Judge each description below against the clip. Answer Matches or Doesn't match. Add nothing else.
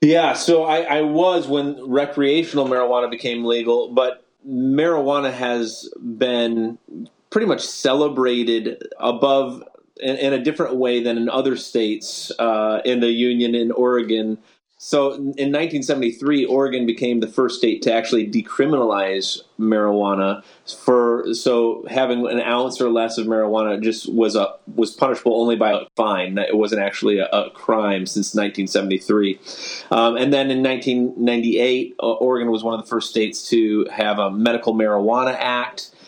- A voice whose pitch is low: Matches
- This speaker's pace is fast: Doesn't match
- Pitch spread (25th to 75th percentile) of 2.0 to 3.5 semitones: Matches